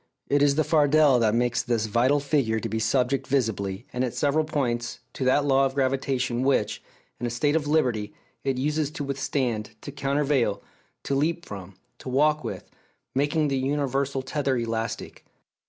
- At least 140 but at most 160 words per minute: No, average, 170 wpm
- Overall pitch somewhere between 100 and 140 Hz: Yes, low, 135 Hz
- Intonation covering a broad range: No, average, 3.4 semitones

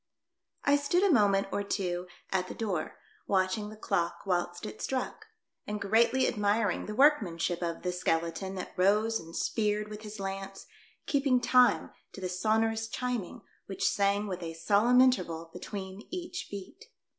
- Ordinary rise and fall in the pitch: Yes, average, 3.6 semitones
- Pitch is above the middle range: Yes, high, 205 Hz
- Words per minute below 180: Yes, average, 160 wpm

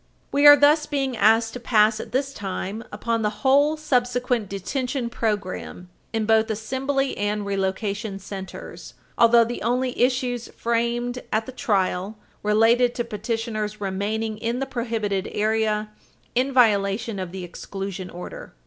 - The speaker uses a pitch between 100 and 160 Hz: No, high, 225 Hz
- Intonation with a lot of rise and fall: No, average, 3.3 semitones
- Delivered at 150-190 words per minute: No, average, 140 wpm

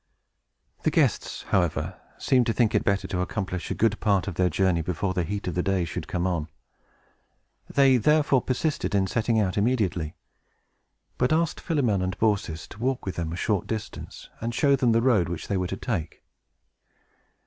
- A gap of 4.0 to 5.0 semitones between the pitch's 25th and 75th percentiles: Yes, average, 4.6 semitones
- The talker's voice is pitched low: Yes, low, 100 Hz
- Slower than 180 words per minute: No, average, 190 wpm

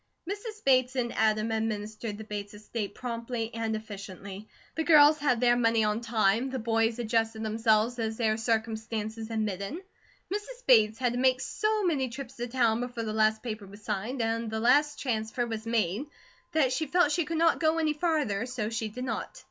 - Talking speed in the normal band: Yes, average, 190 wpm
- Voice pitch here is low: No, high, 230 Hz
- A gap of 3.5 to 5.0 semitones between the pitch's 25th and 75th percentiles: No, average, 2.9 semitones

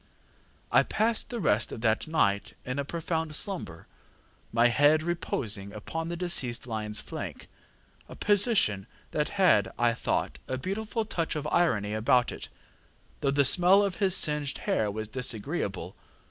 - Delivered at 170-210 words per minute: No, average, 150 wpm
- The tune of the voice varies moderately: No, wide, 8.0 semitones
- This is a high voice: No, medium, 140 Hz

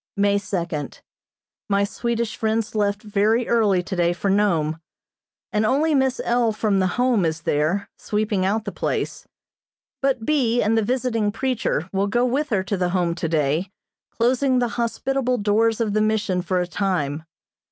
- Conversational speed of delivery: Yes, average, 165 wpm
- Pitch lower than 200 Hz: No, high, 210 Hz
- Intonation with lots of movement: No, average, 4.0 semitones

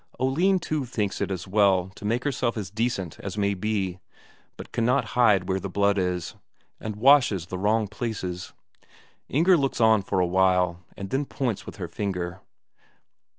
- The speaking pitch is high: No, low, 100 Hz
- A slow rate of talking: No, average, 170 wpm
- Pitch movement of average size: Yes, average, 4.3 semitones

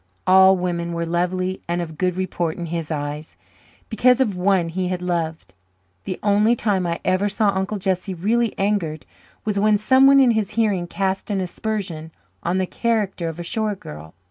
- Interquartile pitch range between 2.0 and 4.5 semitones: Yes, average, 3.4 semitones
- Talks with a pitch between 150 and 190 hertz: Yes, medium, 185 Hz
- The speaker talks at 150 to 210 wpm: Yes, average, 180 wpm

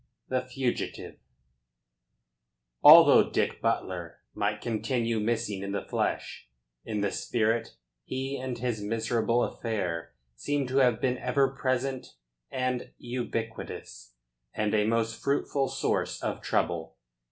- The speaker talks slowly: Yes, slow, 120 wpm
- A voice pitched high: No, low, 115 Hz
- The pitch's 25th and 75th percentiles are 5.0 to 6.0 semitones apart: No, average, 3.2 semitones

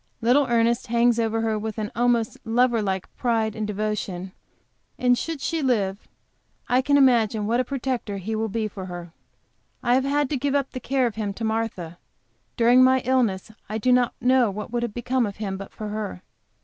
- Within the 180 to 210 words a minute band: Yes, average, 200 wpm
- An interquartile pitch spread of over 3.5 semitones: No, average, 3.0 semitones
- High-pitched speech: Yes, high, 230 Hz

